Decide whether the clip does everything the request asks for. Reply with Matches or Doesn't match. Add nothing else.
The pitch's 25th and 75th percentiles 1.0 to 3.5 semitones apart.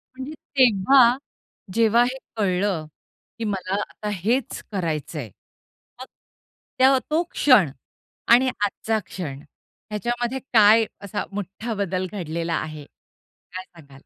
Doesn't match